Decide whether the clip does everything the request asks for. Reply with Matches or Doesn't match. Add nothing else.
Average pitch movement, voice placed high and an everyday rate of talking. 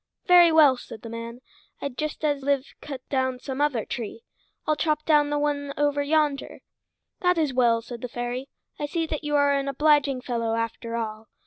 Matches